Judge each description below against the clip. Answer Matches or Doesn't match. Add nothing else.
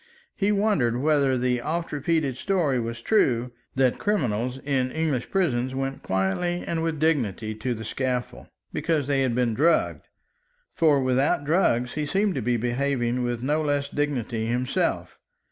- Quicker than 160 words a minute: Doesn't match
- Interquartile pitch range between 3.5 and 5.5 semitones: Matches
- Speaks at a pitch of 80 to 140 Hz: Matches